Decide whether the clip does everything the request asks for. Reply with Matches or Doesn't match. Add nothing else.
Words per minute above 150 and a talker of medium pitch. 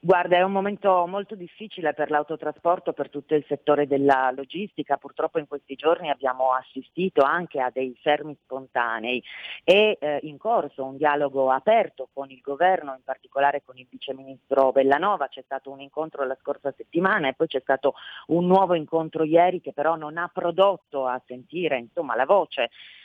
Matches